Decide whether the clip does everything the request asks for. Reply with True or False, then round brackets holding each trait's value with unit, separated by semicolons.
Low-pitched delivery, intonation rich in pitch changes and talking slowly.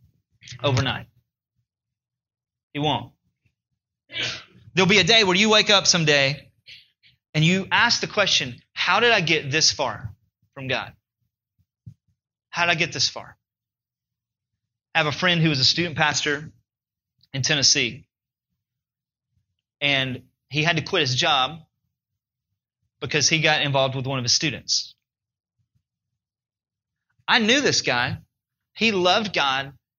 False (130 Hz; 4.5 semitones; 130 wpm)